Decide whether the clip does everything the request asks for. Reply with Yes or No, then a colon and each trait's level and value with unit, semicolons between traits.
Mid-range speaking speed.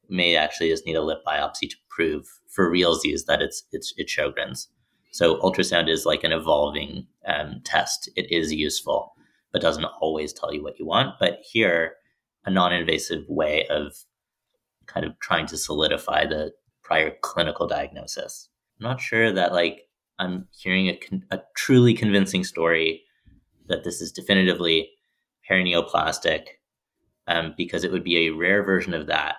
Yes: average, 155 wpm